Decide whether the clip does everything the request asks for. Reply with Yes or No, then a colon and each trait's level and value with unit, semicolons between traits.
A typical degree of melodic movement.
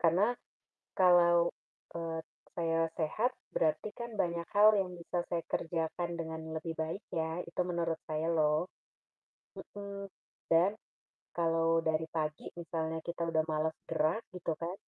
No: narrow, 1.6 semitones